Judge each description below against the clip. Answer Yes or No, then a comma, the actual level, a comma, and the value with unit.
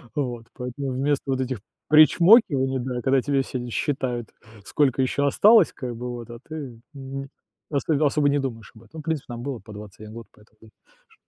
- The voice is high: No, low, 130 Hz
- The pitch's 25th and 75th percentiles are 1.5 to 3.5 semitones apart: Yes, average, 3.1 semitones